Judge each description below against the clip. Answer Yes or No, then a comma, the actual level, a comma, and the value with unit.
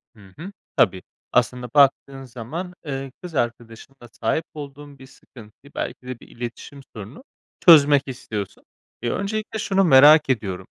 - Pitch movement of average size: Yes, average, 4.1 semitones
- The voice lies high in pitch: No, low, 135 Hz